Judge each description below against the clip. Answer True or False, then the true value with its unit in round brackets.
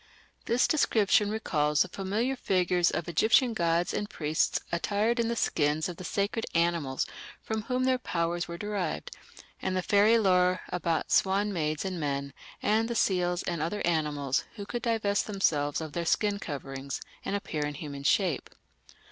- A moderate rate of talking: True (165 wpm)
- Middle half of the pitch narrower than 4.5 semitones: False (4.9 semitones)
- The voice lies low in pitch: False (180 Hz)